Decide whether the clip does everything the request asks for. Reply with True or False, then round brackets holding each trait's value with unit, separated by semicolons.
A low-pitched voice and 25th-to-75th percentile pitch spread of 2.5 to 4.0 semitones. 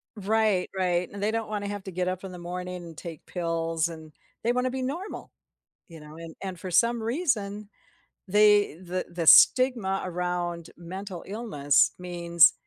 False (185 Hz; 3.6 semitones)